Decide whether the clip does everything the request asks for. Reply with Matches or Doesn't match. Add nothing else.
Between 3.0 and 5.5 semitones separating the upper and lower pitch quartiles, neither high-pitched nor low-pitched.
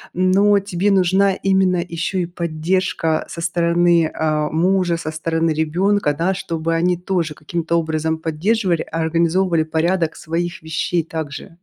Doesn't match